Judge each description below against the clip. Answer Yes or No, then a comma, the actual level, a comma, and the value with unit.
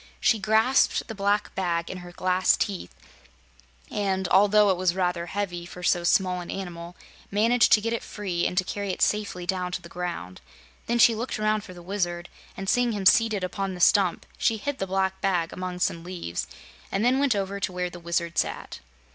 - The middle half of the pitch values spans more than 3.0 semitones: No, average, 2.7 semitones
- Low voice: No, high, 190 Hz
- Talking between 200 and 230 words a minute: Yes, fast, 205 wpm